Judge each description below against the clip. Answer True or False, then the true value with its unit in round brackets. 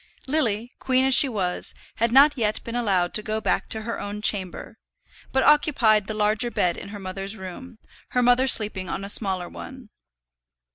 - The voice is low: False (220 Hz)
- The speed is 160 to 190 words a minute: True (185 wpm)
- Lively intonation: False (3.8 semitones)